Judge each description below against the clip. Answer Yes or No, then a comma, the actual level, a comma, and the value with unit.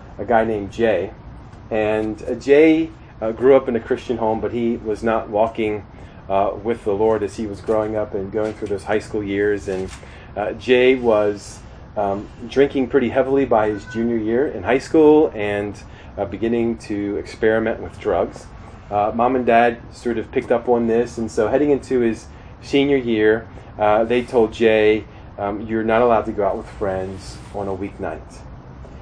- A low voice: Yes, low, 110 Hz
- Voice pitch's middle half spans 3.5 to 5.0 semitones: No, narrow, 2.4 semitones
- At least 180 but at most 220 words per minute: Yes, average, 185 wpm